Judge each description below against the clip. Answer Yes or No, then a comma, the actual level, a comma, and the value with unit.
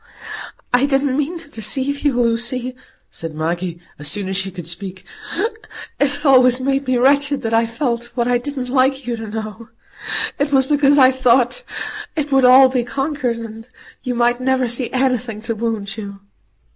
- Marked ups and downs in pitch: No, average, 3.1 semitones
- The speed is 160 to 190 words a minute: Yes, average, 175 wpm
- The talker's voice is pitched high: Yes, very high, 250 Hz